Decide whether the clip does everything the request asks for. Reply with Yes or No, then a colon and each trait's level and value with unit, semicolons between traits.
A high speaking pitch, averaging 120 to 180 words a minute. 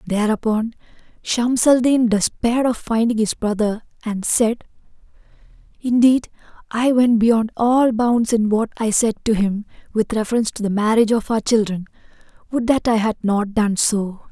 Yes: high, 225 Hz; average, 160 wpm